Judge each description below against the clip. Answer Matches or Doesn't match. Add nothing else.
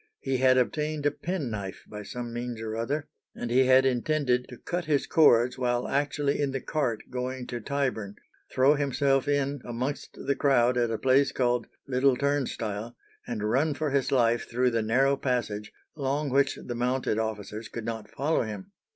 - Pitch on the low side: Matches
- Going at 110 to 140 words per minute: Doesn't match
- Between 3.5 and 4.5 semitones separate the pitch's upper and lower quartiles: Doesn't match